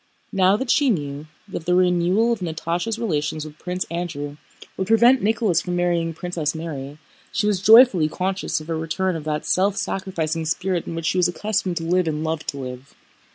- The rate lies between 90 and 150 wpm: No, average, 195 wpm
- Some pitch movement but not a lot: Yes, average, 3.5 semitones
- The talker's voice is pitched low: No, medium, 175 Hz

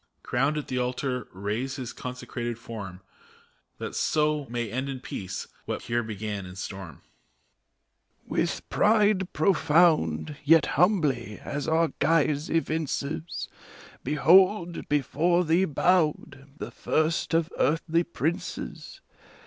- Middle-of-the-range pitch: Yes, medium, 145 Hz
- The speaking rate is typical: No, slow, 120 wpm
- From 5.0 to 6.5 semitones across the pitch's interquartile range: Yes, wide, 5.6 semitones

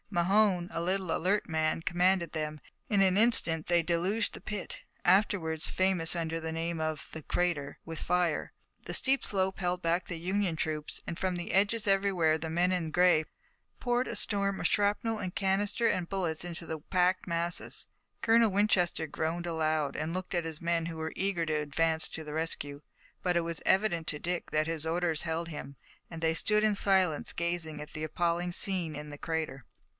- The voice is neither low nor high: Yes, medium, 170 Hz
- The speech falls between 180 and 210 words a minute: Yes, average, 190 wpm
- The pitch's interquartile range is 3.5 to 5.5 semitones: No, average, 2.9 semitones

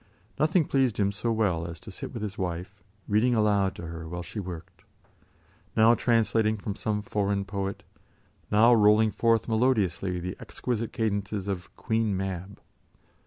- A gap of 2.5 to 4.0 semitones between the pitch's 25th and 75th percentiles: Yes, average, 2.8 semitones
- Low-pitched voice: Yes, low, 105 Hz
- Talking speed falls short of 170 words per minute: Yes, average, 155 wpm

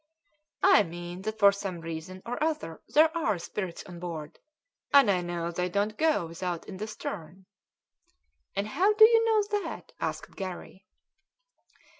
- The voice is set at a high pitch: Yes, high, 195 Hz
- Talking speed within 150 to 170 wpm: Yes, average, 155 wpm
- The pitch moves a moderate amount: No, wide, 7.9 semitones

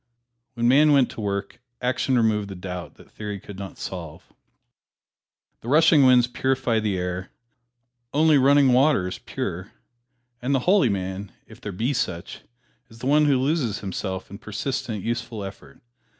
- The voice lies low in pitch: Yes, low, 115 Hz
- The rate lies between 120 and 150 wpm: No, average, 160 wpm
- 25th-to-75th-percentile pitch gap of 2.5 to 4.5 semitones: No, average, 5.3 semitones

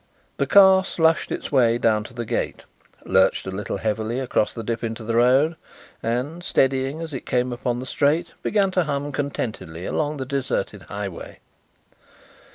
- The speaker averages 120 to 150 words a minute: No, average, 165 wpm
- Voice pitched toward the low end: Yes, low, 130 Hz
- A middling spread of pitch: Yes, average, 4.6 semitones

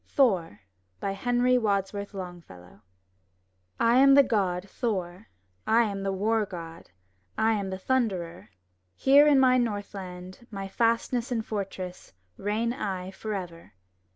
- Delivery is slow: Yes, slow, 125 wpm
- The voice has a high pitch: Yes, high, 200 Hz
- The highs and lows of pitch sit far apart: No, average, 4.1 semitones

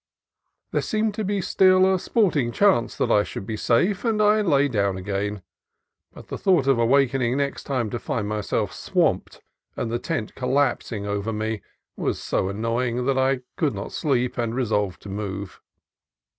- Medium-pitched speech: No, low, 125 Hz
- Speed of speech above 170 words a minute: Yes, average, 180 wpm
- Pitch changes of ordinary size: No, wide, 6.2 semitones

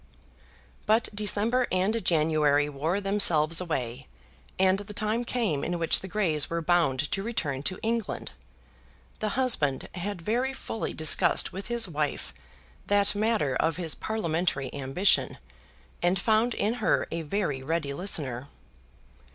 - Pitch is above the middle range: No, medium, 180 Hz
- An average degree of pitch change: No, wide, 5.8 semitones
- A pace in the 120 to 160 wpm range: Yes, slow, 135 wpm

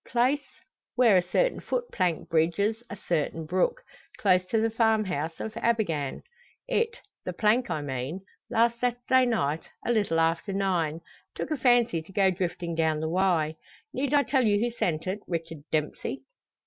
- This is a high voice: Yes, high, 195 Hz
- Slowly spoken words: No, average, 165 wpm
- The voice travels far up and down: Yes, wide, 6.4 semitones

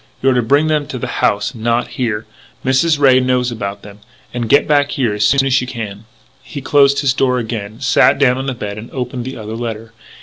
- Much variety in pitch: No, average, 3.3 semitones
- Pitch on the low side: Yes, low, 125 Hz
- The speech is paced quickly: Yes, fast, 225 wpm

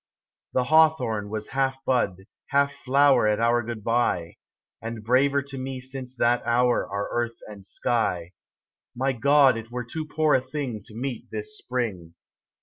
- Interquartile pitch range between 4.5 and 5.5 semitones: No, average, 3.4 semitones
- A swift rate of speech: No, average, 155 wpm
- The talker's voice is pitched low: Yes, low, 125 Hz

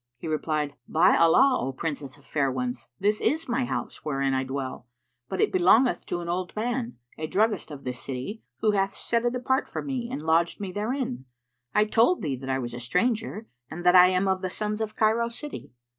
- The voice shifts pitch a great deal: Yes, wide, 8.0 semitones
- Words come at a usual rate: No, fast, 215 wpm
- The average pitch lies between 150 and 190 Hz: Yes, medium, 185 Hz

